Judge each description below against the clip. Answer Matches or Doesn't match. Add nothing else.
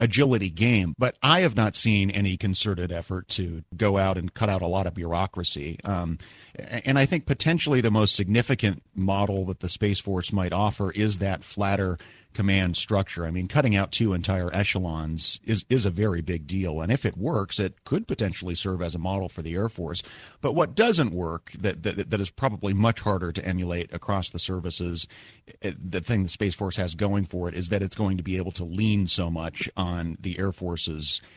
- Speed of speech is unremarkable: Doesn't match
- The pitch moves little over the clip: Doesn't match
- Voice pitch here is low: Matches